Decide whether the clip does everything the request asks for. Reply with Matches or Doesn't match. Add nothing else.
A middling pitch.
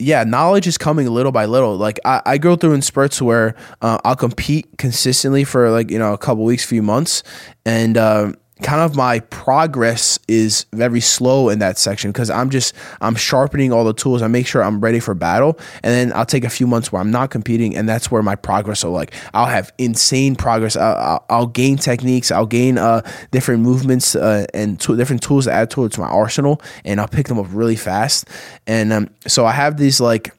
Doesn't match